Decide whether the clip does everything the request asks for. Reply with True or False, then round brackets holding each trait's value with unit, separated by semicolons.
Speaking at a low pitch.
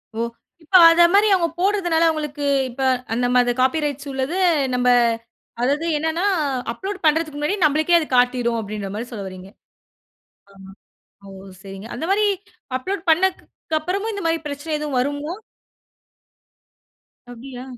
False (295 Hz)